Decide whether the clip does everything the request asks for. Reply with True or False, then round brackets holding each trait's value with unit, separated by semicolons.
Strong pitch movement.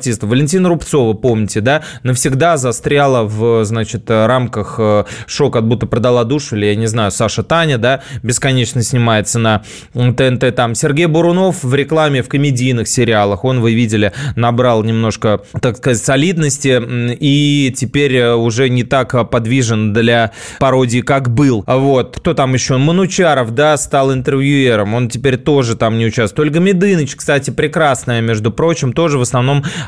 False (3.6 semitones)